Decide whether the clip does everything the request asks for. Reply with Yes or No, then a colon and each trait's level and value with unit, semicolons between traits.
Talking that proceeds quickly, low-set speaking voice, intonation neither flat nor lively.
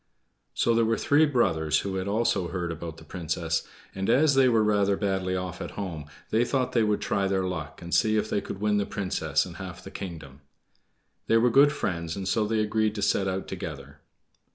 Yes: fast, 215 wpm; very low, 95 Hz; average, 4.2 semitones